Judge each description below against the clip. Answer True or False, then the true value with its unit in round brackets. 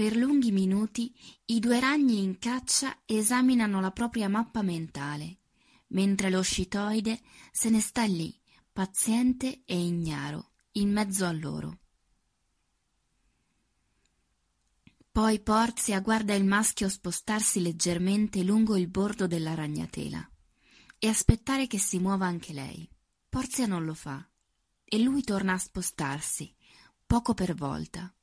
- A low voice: False (200 Hz)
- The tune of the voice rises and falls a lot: False (4.6 semitones)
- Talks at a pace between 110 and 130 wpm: True (125 wpm)